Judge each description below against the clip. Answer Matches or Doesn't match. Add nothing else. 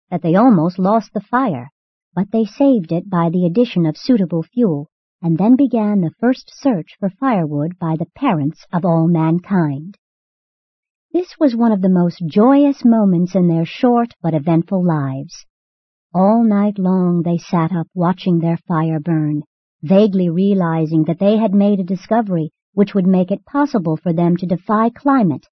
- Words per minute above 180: Doesn't match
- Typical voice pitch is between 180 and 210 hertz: Matches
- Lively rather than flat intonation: Doesn't match